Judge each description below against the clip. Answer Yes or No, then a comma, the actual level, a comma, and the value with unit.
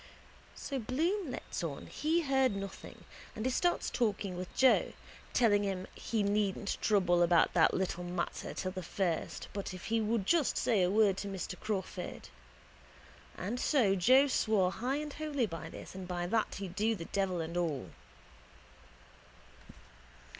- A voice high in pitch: Yes, high, 200 Hz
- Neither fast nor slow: Yes, average, 160 wpm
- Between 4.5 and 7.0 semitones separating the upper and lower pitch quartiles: Yes, average, 5.2 semitones